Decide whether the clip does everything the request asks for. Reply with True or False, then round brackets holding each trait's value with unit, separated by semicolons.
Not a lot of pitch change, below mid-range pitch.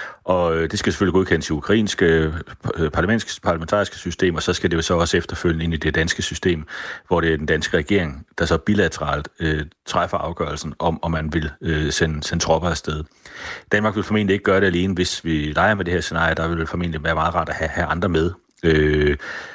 True (2.2 semitones; 85 Hz)